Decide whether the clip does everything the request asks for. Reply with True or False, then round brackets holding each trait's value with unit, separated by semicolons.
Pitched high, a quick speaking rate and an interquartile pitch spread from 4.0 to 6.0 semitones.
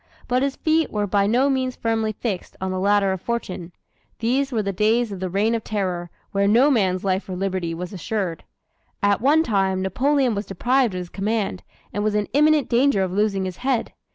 True (205 Hz; 210 wpm; 4.3 semitones)